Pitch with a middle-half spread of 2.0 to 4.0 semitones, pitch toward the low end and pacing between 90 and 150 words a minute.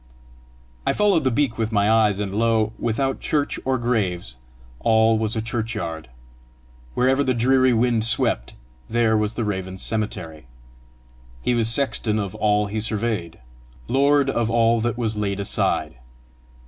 Yes: narrow, 2.5 semitones; low, 110 Hz; average, 145 wpm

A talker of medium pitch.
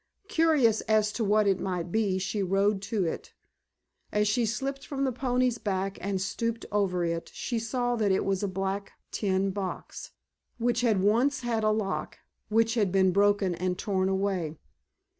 No: high, 205 Hz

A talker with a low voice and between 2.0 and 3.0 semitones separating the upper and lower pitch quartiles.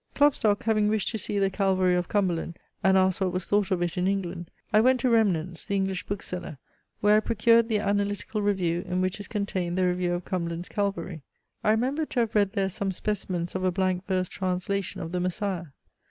No: high, 190 Hz; narrow, 2.5 semitones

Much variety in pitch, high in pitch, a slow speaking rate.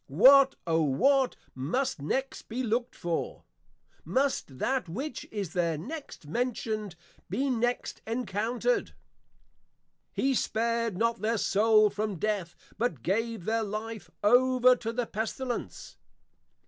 No: average, 4.1 semitones; high, 225 Hz; slow, 120 wpm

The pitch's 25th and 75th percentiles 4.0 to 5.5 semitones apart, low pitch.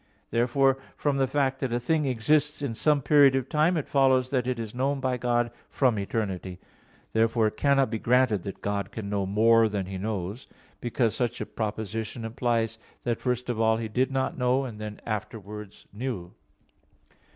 No: average, 3.6 semitones; low, 120 Hz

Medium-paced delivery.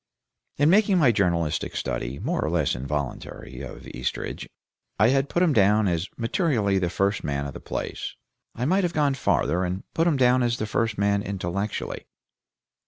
Yes: average, 175 wpm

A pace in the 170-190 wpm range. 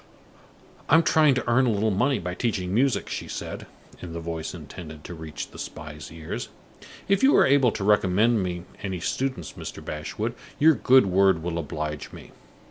Yes: average, 185 wpm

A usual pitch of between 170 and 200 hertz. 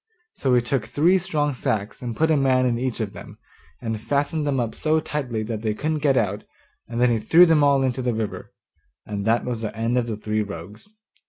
No: low, 125 Hz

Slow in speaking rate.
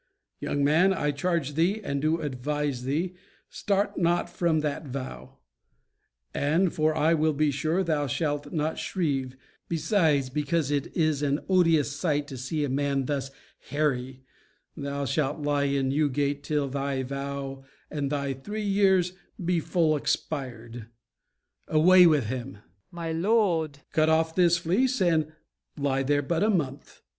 No: average, 150 wpm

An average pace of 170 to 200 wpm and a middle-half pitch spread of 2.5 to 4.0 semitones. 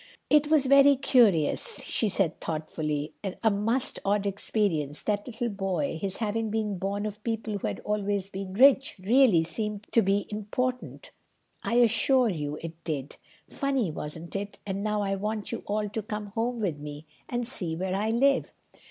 Yes: average, 180 wpm; average, 3.7 semitones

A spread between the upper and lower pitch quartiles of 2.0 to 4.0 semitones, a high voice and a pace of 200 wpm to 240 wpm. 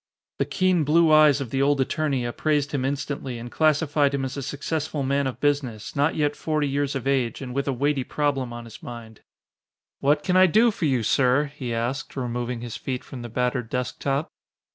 No: average, 2.8 semitones; medium, 140 Hz; fast, 205 wpm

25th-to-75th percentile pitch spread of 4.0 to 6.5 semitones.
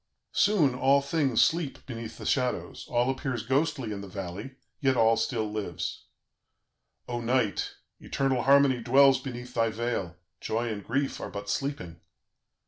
No: average, 3.5 semitones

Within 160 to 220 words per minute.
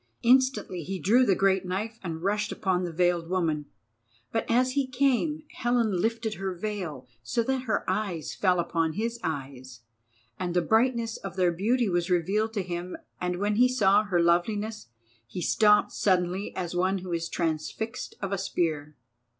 Yes: average, 170 wpm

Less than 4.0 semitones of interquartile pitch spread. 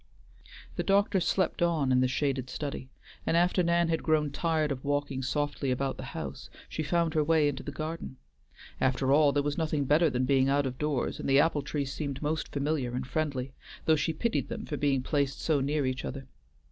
Yes: narrow, 2.6 semitones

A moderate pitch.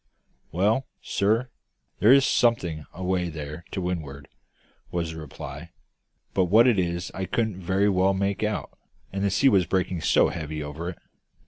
No: very low, 95 Hz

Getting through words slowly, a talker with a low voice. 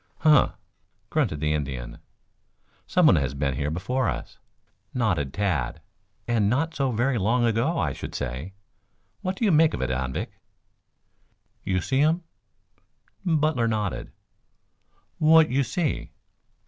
Yes: slow, 130 wpm; low, 115 Hz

